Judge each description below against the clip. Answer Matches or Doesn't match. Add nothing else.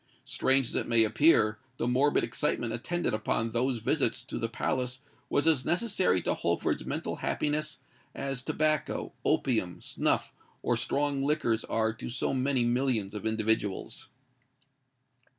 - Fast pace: Doesn't match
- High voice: Doesn't match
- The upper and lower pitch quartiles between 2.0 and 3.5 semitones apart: Doesn't match